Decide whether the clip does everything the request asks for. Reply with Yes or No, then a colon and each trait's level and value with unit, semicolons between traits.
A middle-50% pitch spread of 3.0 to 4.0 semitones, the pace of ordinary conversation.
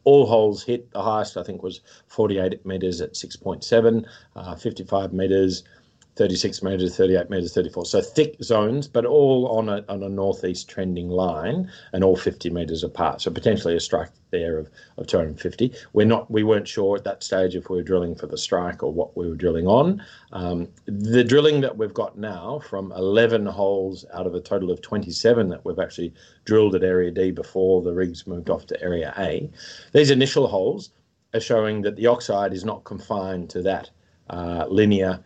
Yes: average, 3.7 semitones; average, 190 wpm